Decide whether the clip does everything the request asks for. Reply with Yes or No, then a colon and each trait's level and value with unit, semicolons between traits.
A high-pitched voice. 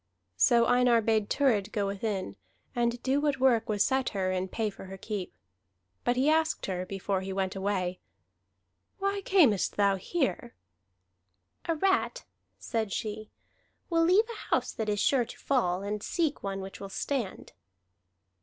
Yes: high, 220 Hz